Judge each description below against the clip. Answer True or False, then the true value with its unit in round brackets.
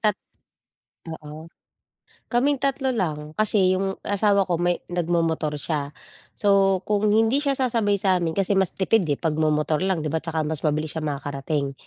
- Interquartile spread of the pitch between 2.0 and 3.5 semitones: False (4.7 semitones)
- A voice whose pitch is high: False (175 Hz)